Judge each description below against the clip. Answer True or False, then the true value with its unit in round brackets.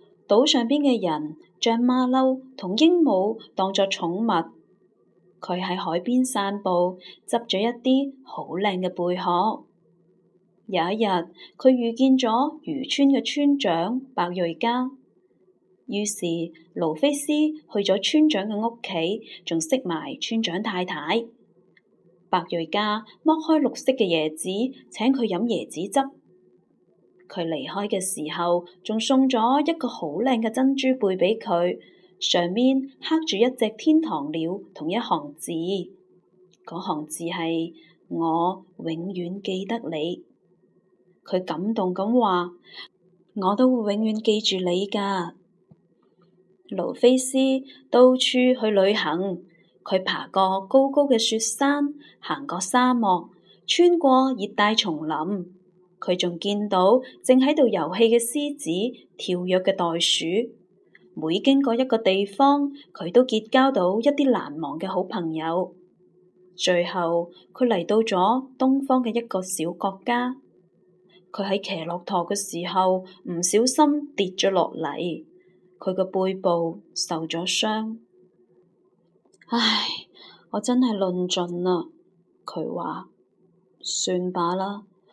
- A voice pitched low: False (195 Hz)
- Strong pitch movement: True (5.8 semitones)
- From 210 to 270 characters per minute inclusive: False (175 characters per minute)